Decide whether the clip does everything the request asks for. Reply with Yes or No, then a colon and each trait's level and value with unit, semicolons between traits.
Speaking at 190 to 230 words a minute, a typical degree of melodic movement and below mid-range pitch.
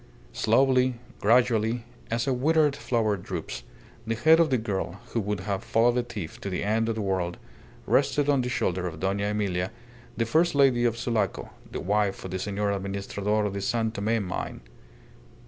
No: average, 180 wpm; average, 3.6 semitones; low, 110 Hz